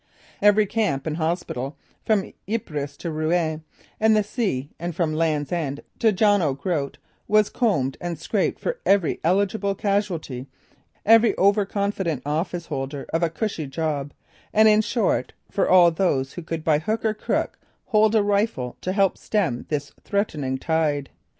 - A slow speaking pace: No, average, 155 wpm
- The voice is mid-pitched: Yes, medium, 175 Hz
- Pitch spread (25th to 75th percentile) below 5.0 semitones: No, wide, 5.6 semitones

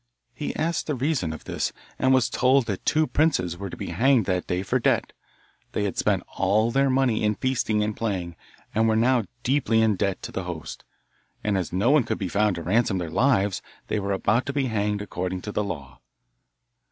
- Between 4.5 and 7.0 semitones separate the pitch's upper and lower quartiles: Yes, wide, 5.4 semitones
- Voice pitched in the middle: No, low, 105 Hz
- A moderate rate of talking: No, fast, 215 wpm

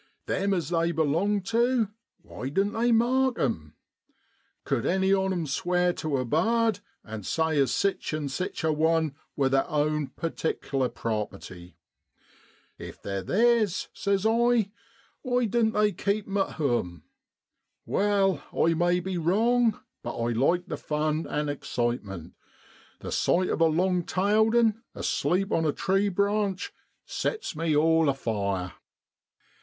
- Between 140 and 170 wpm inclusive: Yes, average, 145 wpm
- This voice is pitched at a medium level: Yes, medium, 175 Hz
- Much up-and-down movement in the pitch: Yes, wide, 6.2 semitones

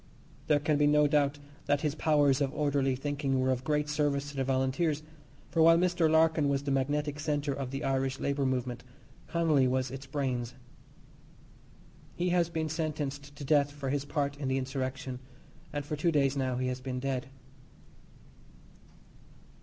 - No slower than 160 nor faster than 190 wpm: Yes, average, 170 wpm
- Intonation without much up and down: Yes, narrow, 2.0 semitones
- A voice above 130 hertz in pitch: Yes, medium, 140 Hz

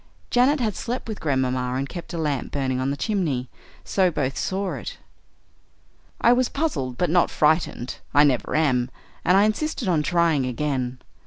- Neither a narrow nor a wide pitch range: No, wide, 7.0 semitones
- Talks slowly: No, average, 170 wpm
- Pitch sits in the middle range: Yes, medium, 155 Hz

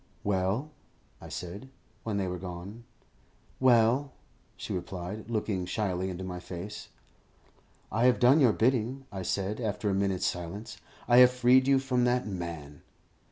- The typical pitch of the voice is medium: No, low, 105 Hz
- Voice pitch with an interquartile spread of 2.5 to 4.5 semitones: No, average, 5.1 semitones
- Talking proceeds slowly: No, average, 150 wpm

